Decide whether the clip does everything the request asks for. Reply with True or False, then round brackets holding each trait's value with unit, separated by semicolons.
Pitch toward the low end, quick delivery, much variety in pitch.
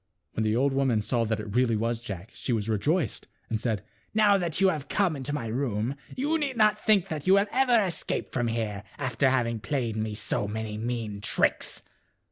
True (120 Hz; 210 wpm; 7.4 semitones)